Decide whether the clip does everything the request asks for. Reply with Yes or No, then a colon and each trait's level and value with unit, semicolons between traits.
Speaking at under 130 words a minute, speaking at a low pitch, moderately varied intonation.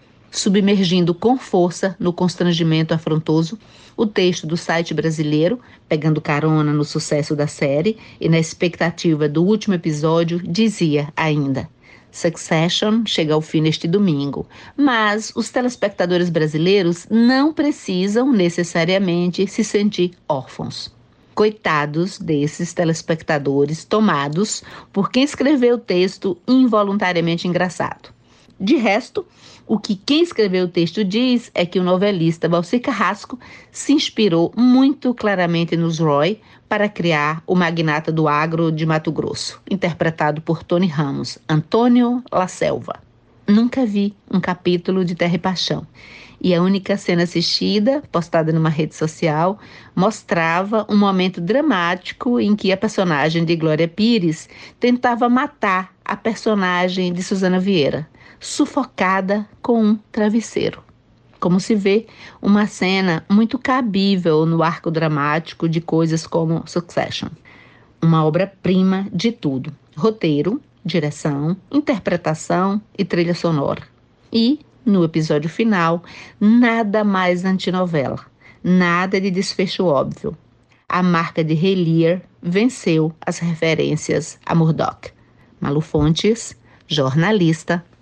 No: slow, 120 wpm; medium, 180 Hz; average, 4.4 semitones